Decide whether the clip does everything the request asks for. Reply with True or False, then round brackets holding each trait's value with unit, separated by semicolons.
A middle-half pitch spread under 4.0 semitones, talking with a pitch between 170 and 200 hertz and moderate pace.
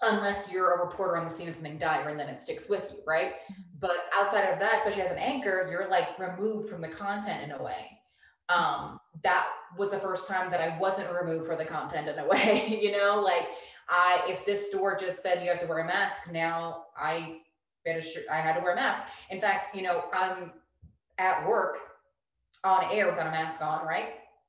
False (3.3 semitones; 185 Hz; 215 wpm)